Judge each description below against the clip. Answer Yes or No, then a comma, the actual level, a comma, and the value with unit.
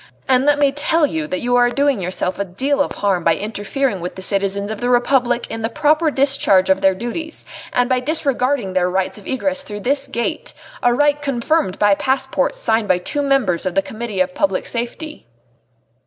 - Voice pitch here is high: Yes, high, 245 Hz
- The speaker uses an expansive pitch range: Yes, wide, 6.0 semitones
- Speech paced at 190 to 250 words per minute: Yes, average, 200 wpm